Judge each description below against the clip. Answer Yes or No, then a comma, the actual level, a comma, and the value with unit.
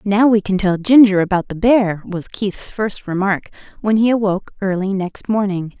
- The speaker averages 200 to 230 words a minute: No, average, 185 wpm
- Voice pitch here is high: Yes, high, 200 Hz